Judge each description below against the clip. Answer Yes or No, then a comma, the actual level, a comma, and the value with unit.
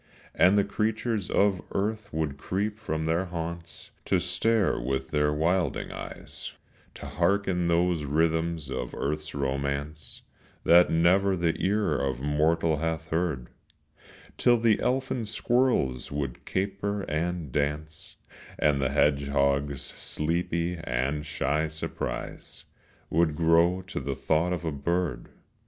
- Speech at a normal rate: No, slow, 125 wpm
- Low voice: Yes, very low, 80 Hz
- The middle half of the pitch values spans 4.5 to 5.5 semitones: No, average, 4.0 semitones